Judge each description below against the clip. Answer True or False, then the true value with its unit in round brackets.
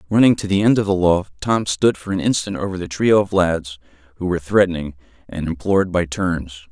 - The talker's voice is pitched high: False (90 Hz)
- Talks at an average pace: False (215 wpm)